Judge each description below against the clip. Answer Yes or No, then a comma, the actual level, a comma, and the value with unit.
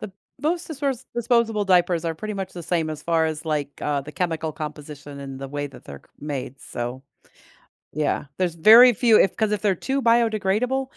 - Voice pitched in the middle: Yes, medium, 175 Hz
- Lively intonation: Yes, wide, 6.8 semitones